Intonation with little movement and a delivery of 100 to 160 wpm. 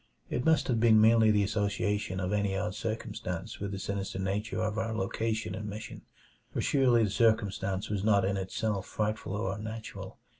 No: narrow, 2.1 semitones; average, 180 wpm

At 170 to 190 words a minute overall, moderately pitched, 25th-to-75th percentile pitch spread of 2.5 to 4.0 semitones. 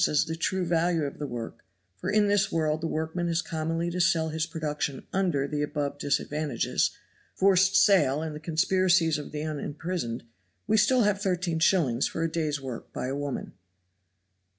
Yes: average, 175 wpm; medium, 160 Hz; average, 3.3 semitones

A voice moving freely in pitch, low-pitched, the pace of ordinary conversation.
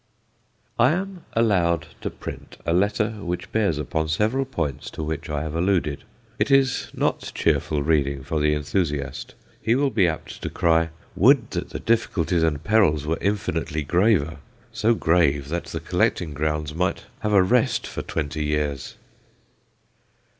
Yes: wide, 5.8 semitones; very low, 80 Hz; average, 155 wpm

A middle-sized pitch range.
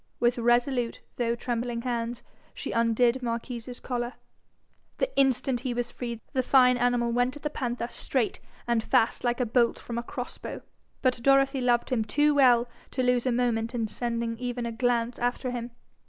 No: narrow, 1.2 semitones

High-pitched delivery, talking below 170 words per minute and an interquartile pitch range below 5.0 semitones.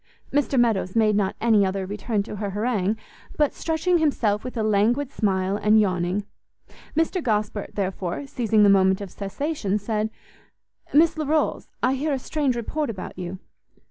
No: high, 215 Hz; average, 160 wpm; wide, 5.5 semitones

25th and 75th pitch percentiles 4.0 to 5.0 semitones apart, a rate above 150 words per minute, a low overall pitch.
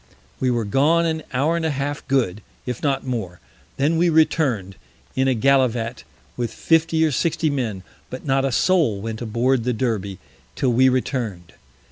Yes: average, 4.5 semitones; average, 170 wpm; low, 130 Hz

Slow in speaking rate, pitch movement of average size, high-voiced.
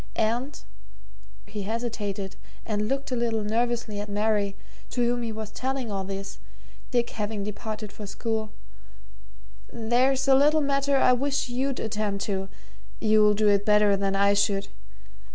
No: average, 150 wpm; average, 3.0 semitones; high, 220 Hz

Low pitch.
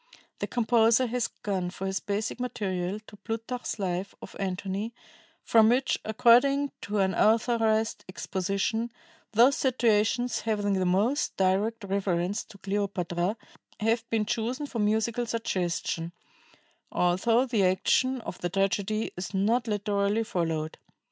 No: high, 210 Hz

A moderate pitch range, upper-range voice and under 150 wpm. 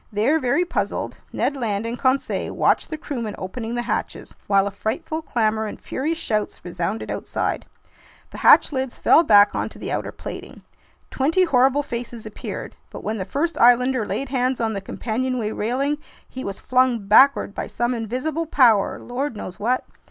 No: average, 4.0 semitones; high, 245 Hz; average, 170 wpm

